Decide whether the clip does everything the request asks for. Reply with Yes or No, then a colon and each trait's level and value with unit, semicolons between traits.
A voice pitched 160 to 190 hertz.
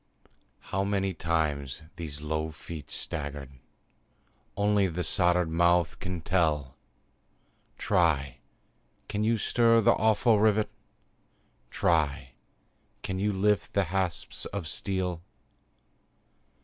No: very low, 90 Hz